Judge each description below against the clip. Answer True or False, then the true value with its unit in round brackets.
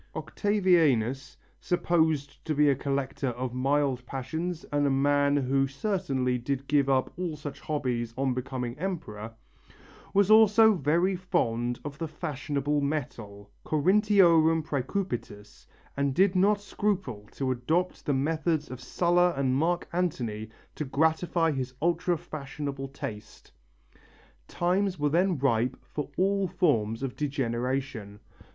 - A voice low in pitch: False (145 Hz)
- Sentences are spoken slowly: True (130 wpm)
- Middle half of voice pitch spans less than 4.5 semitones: False (5.1 semitones)